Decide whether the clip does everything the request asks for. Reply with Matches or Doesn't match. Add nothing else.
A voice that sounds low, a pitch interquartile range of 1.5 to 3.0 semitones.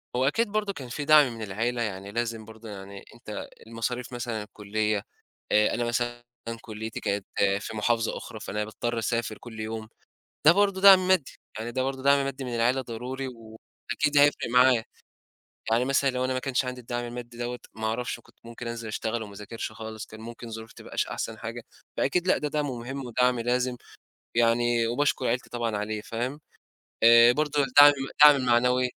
Matches